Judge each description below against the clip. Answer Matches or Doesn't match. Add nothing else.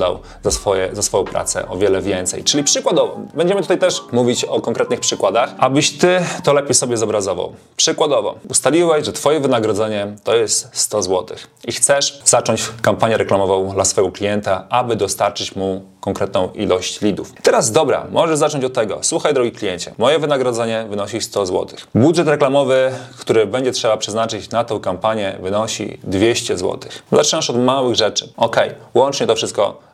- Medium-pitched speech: Doesn't match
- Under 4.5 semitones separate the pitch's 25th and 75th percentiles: Doesn't match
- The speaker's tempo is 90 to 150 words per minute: Doesn't match